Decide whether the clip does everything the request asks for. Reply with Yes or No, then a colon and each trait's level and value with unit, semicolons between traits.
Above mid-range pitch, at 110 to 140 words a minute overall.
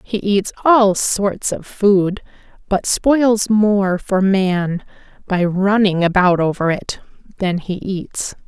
Yes: high, 195 Hz; slow, 135 wpm